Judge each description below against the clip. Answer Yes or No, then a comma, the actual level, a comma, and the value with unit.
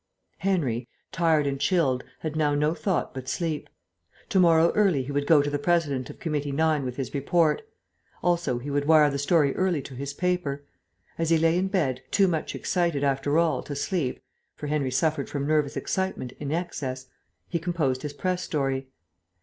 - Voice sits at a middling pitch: Yes, medium, 150 Hz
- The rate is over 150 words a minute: Yes, average, 185 wpm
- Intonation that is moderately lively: Yes, average, 3.4 semitones